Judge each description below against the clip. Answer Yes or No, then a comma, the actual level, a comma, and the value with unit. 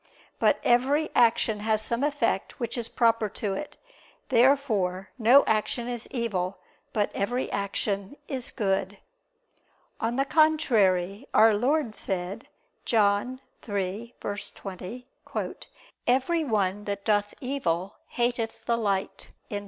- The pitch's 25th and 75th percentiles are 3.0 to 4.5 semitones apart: Yes, average, 3.9 semitones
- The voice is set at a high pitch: Yes, high, 225 Hz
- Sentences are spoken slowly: Yes, slow, 115 wpm